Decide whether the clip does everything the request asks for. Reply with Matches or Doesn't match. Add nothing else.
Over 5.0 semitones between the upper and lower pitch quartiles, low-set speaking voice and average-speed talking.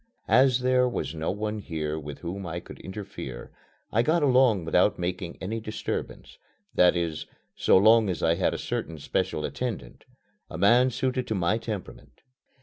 Matches